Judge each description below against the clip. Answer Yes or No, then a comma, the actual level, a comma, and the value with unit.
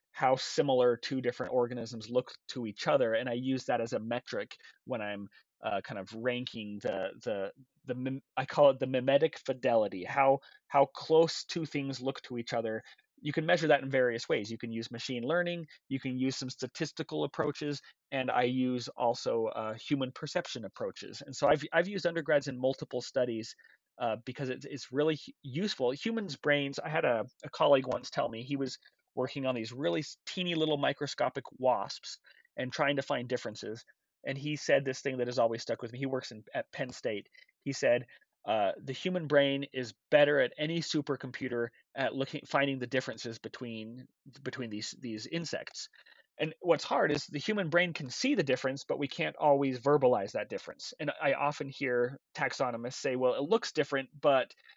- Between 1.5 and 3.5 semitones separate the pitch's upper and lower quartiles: Yes, average, 3.1 semitones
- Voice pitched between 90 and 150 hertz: Yes, low, 135 Hz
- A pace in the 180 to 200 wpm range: Yes, average, 190 wpm